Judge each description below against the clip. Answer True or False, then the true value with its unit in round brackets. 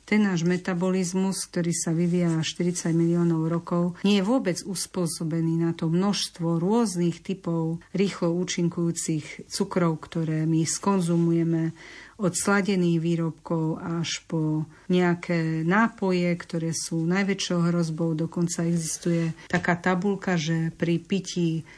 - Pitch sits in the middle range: True (170 Hz)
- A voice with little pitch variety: True (1.8 semitones)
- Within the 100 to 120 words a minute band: True (115 wpm)